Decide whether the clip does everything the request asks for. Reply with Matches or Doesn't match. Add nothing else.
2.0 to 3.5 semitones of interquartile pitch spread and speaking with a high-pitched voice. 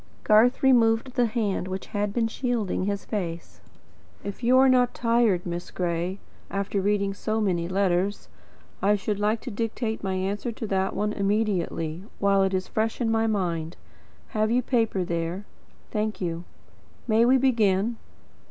Matches